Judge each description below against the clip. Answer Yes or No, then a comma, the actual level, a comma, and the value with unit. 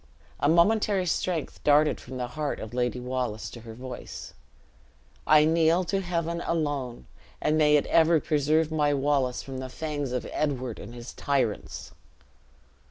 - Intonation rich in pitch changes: No, average, 4.1 semitones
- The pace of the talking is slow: No, average, 155 wpm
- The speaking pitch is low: No, medium, 145 Hz